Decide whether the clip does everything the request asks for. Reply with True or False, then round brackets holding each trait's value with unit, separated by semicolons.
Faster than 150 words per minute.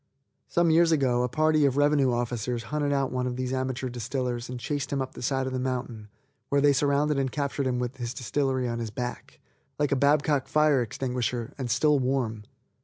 True (205 wpm)